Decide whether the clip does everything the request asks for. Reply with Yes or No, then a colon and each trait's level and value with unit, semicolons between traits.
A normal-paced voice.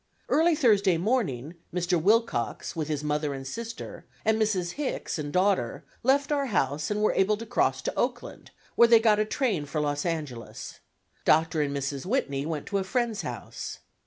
Yes: average, 180 wpm